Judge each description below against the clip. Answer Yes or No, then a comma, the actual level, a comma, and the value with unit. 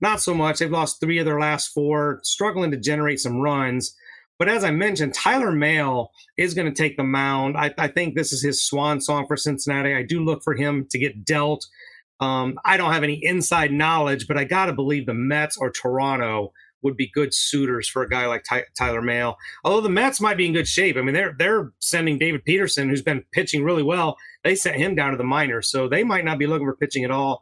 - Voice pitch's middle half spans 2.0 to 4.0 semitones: Yes, average, 3.1 semitones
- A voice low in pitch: No, medium, 145 Hz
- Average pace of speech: No, fast, 235 wpm